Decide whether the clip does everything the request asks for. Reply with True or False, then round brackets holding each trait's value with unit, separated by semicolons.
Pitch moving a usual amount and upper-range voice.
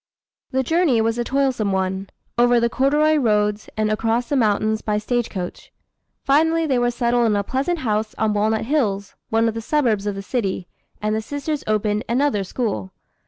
True (3.9 semitones; 225 Hz)